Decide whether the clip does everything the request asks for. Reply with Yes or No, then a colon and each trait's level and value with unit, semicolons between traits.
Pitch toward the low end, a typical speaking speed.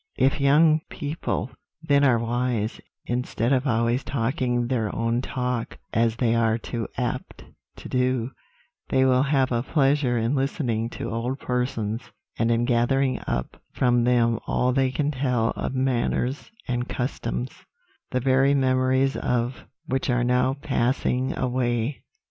Yes: low, 125 Hz; average, 145 wpm